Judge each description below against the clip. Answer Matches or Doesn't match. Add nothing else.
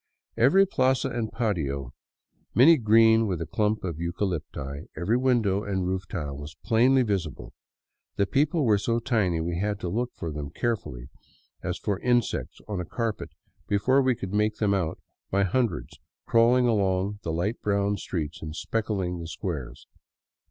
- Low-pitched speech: Matches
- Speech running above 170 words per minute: Doesn't match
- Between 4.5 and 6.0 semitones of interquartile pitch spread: Matches